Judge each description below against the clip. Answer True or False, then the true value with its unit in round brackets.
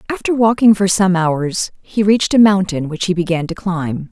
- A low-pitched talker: False (190 Hz)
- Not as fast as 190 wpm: False (205 wpm)